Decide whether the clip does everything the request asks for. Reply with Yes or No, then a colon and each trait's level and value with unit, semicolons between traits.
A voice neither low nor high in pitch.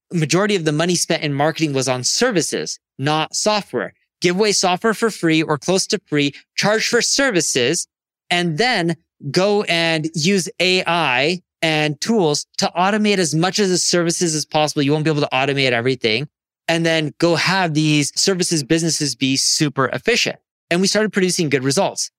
Yes: medium, 165 Hz